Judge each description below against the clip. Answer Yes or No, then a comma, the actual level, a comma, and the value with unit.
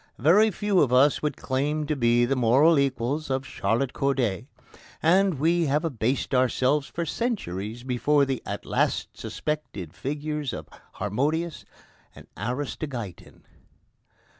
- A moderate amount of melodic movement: Yes, average, 4.0 semitones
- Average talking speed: No, slow, 130 wpm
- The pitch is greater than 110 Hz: Yes, medium, 140 Hz